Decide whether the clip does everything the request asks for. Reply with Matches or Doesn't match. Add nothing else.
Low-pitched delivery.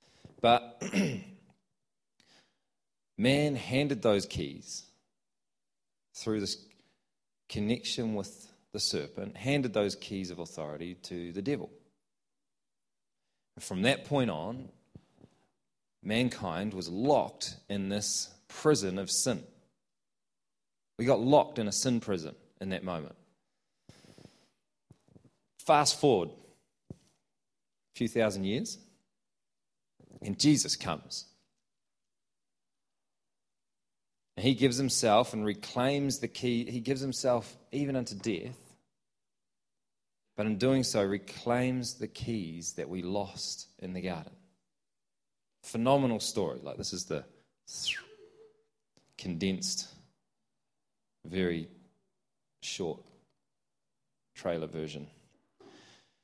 Matches